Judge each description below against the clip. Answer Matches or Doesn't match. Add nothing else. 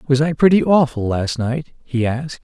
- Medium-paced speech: Matches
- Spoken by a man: Matches